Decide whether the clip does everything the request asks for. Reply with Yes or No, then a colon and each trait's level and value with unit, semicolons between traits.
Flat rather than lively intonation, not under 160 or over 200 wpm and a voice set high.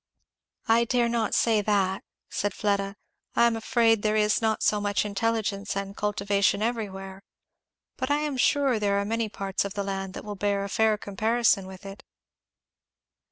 Yes: narrow, 2.3 semitones; average, 170 wpm; high, 210 Hz